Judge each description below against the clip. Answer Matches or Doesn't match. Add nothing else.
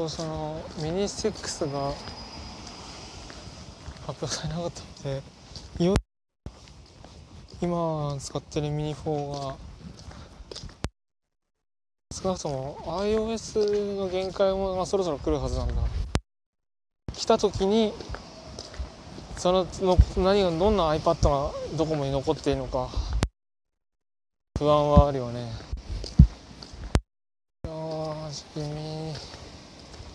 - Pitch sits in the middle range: Matches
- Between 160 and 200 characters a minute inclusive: Matches